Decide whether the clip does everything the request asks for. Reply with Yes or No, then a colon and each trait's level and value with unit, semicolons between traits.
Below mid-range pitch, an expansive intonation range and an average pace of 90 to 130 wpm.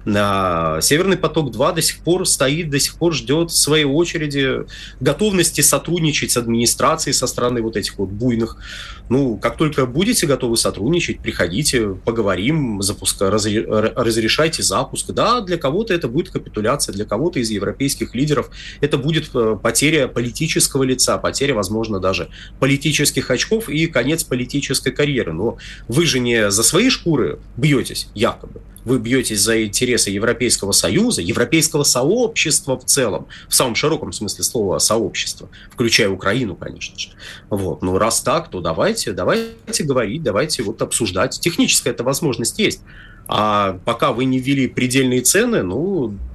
No: low, 130 Hz; wide, 6.0 semitones; average, 145 wpm